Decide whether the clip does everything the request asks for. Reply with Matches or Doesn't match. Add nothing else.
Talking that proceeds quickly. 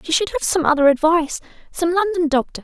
Doesn't match